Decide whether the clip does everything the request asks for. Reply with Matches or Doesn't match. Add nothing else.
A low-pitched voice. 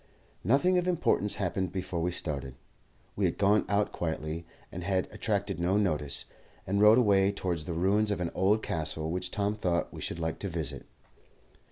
Matches